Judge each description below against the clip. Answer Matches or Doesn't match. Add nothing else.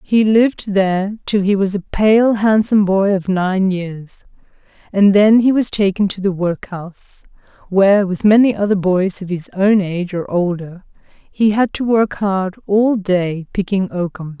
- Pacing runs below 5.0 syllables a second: Matches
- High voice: Matches